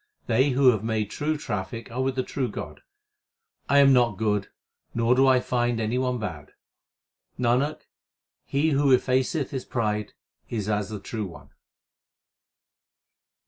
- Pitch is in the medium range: No, low, 120 Hz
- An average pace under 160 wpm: Yes, average, 145 wpm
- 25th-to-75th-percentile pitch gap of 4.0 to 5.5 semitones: No, average, 3.6 semitones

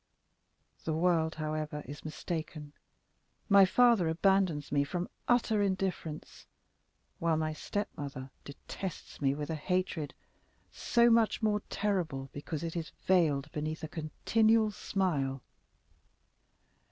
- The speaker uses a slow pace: Yes, slow, 115 wpm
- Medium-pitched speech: Yes, medium, 160 Hz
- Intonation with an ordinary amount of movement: Yes, average, 4.5 semitones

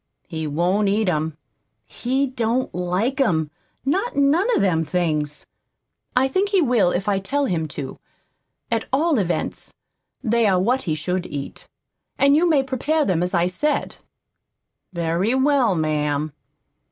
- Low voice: No, high, 200 Hz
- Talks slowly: No, average, 150 wpm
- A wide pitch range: Yes, wide, 8.1 semitones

